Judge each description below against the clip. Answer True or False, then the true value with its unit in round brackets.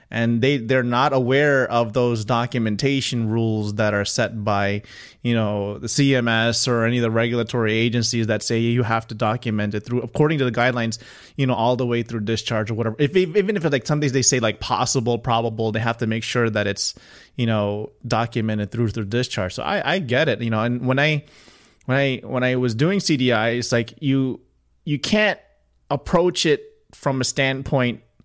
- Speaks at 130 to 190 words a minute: False (205 wpm)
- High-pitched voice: False (120 Hz)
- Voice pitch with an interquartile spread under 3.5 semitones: True (2.9 semitones)